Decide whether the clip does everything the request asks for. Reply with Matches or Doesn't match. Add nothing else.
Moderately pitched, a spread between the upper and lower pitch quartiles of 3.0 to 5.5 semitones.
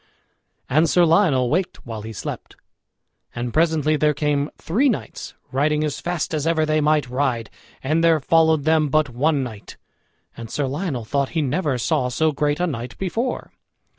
Matches